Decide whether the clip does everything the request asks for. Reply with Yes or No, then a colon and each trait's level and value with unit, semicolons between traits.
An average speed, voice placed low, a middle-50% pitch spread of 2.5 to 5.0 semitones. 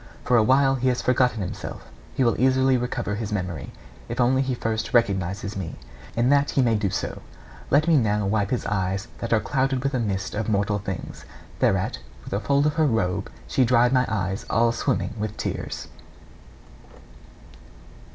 Yes: average, 180 wpm; low, 115 Hz; average, 4.3 semitones